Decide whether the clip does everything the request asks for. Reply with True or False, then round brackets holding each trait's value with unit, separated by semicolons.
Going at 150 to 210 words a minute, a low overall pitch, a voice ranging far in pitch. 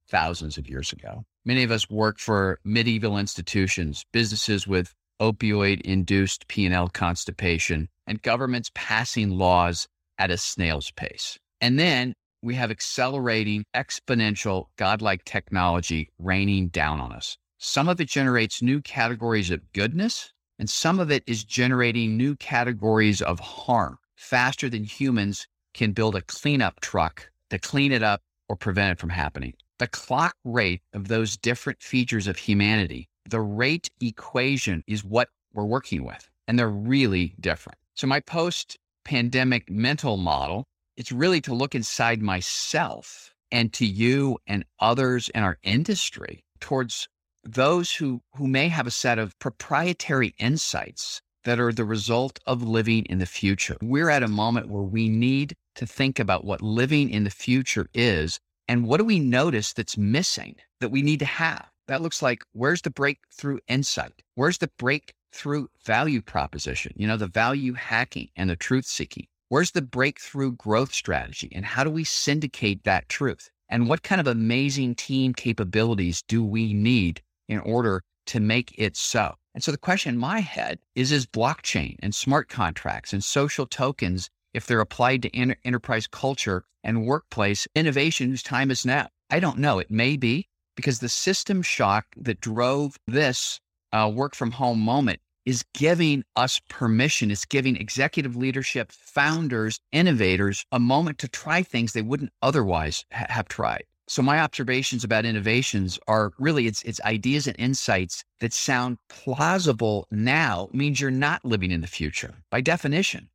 False (160 wpm; 120 Hz; 4.8 semitones)